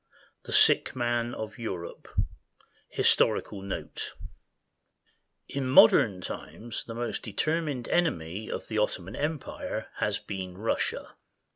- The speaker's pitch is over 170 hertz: No, low, 115 Hz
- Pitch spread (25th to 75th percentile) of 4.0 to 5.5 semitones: Yes, average, 4.8 semitones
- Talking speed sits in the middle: No, slow, 120 wpm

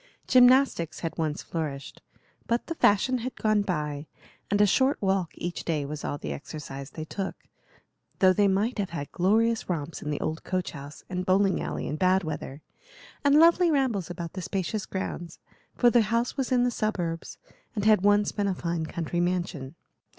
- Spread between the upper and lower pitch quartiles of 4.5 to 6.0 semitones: Yes, average, 5.2 semitones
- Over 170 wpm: Yes, average, 185 wpm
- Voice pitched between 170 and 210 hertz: Yes, medium, 185 Hz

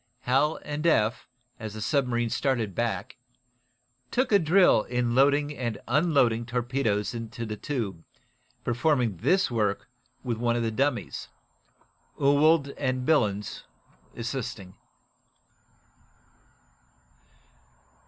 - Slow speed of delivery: Yes, slow, 105 wpm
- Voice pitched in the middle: No, low, 125 Hz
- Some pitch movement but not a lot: Yes, average, 4.1 semitones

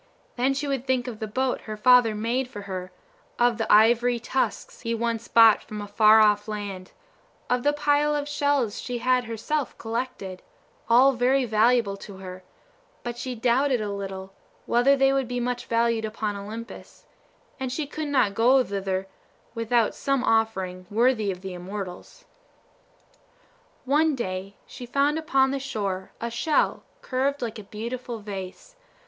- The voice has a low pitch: No, high, 235 Hz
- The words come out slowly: No, average, 160 wpm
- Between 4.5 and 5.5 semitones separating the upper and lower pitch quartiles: No, average, 3.9 semitones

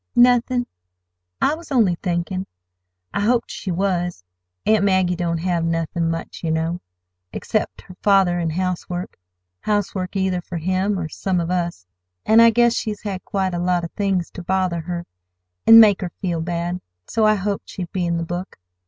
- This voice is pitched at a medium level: Yes, medium, 180 Hz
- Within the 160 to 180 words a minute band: Yes, average, 175 wpm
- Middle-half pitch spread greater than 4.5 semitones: No, average, 2.7 semitones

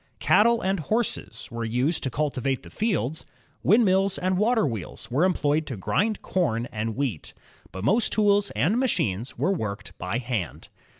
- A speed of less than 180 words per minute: Yes, average, 160 wpm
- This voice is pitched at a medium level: Yes, medium, 150 Hz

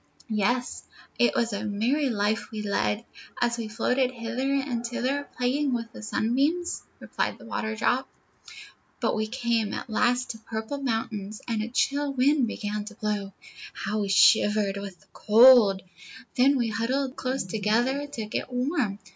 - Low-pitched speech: No, high, 235 Hz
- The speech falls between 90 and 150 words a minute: No, average, 165 wpm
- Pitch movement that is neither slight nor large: Yes, average, 3.4 semitones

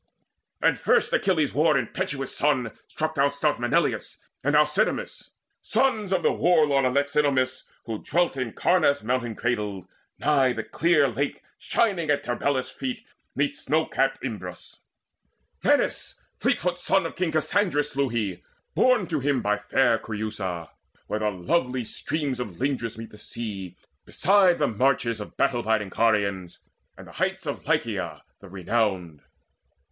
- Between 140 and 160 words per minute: Yes, average, 145 wpm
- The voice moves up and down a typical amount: No, wide, 5.9 semitones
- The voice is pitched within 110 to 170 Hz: Yes, low, 135 Hz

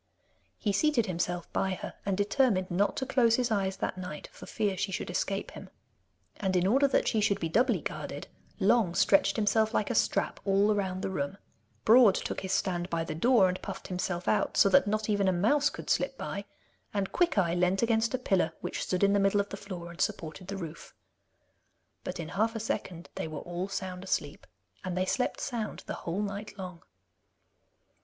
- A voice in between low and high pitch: No, high, 195 Hz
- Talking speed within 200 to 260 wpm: Yes, fast, 205 wpm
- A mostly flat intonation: No, average, 3.0 semitones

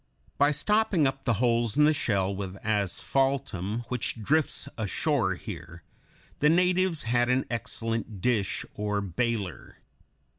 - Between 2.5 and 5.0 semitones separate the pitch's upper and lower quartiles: No, wide, 5.6 semitones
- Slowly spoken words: Yes, slow, 125 wpm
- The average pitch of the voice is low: Yes, low, 115 Hz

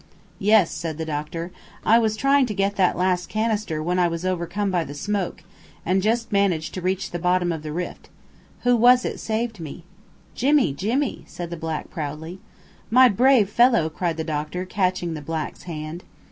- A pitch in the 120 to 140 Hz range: No, medium, 180 Hz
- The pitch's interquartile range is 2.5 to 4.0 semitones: No, average, 4.8 semitones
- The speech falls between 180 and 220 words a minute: Yes, average, 185 wpm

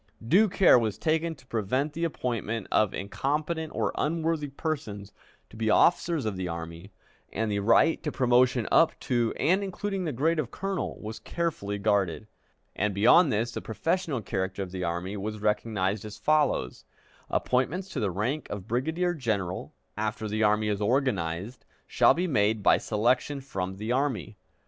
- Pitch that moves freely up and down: Yes, wide, 6.9 semitones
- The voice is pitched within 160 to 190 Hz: No, low, 115 Hz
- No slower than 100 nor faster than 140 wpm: No, average, 165 wpm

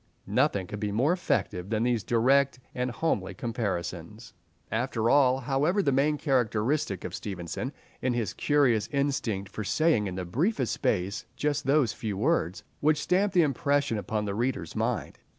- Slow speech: No, average, 160 wpm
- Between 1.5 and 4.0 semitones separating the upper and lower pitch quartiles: No, wide, 5.4 semitones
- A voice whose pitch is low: Yes, low, 120 Hz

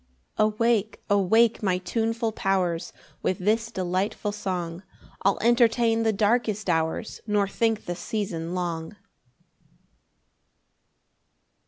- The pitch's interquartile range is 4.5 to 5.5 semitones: No, average, 3.7 semitones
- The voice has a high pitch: Yes, high, 205 Hz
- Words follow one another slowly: Yes, slow, 105 wpm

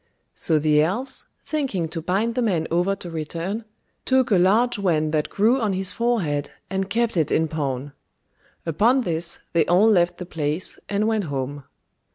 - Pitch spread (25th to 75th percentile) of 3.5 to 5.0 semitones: No, wide, 5.6 semitones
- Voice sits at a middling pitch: Yes, medium, 180 Hz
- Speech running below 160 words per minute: No, average, 175 wpm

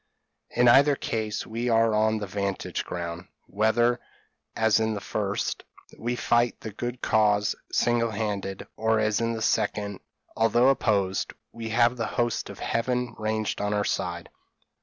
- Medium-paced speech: Yes, average, 155 wpm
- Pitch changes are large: No, narrow, 2.4 semitones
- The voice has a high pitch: No, low, 110 Hz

